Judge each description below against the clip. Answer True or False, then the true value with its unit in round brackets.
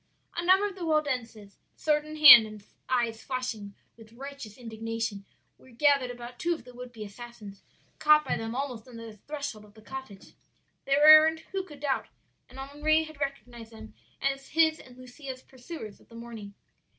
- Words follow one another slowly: False (180 wpm)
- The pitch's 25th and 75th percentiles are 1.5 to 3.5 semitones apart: False (4.8 semitones)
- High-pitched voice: True (255 Hz)